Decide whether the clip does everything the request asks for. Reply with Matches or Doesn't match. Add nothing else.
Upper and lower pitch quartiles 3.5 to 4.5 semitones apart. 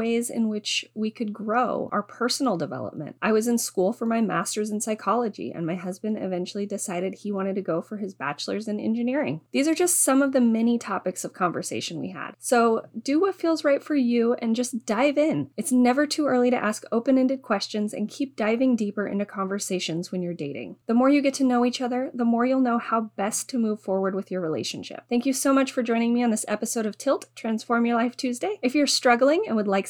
Matches